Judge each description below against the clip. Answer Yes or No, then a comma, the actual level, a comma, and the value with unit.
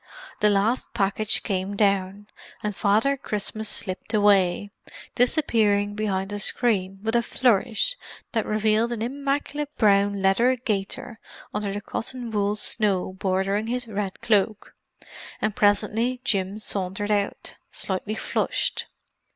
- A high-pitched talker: Yes, high, 210 Hz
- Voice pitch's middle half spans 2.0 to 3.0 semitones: Yes, narrow, 2.4 semitones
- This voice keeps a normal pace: No, slow, 125 wpm